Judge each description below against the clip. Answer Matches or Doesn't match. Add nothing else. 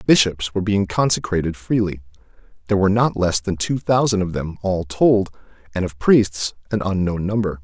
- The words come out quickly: Doesn't match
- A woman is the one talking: Doesn't match